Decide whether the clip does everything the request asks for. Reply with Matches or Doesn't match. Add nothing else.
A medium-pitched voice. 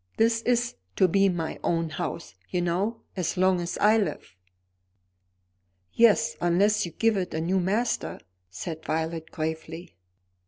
Matches